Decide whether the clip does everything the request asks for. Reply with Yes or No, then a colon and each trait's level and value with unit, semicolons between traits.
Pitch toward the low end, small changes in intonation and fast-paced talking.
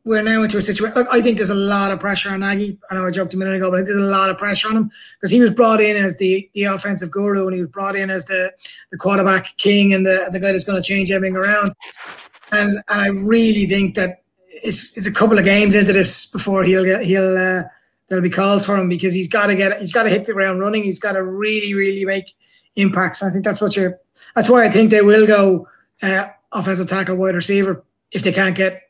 No: high, 195 Hz; narrow, 1.4 semitones; fast, 255 wpm